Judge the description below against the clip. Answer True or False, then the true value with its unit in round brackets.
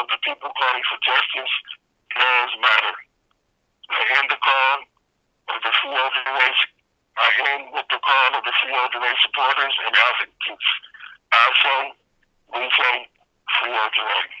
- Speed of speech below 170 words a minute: True (150 wpm)